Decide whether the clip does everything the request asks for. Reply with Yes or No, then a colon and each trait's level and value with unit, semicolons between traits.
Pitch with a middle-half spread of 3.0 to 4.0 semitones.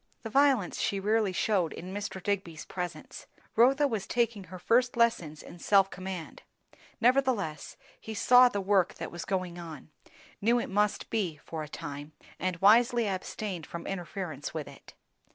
No: average, 4.6 semitones